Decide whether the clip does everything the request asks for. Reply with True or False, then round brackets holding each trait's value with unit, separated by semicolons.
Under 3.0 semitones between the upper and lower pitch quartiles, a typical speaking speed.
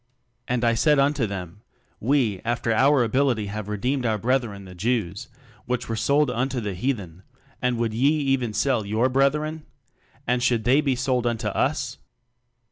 False (3.9 semitones; 170 wpm)